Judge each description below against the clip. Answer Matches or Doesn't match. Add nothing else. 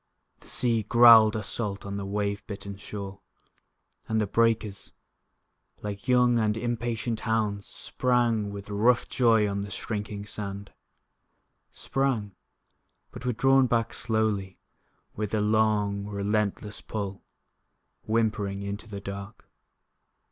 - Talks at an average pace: Doesn't match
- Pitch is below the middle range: Matches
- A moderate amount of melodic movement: Doesn't match